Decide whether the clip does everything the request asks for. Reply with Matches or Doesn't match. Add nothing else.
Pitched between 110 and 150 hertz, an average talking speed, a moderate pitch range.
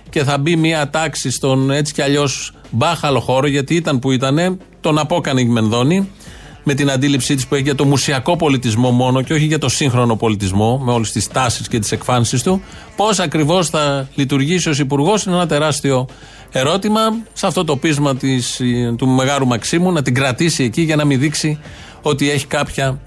Doesn't match